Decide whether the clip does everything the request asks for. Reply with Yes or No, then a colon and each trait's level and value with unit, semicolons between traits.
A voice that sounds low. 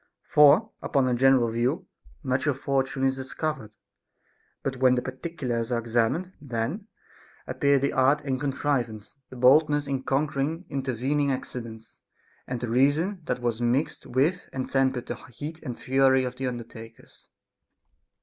Yes: low, 130 Hz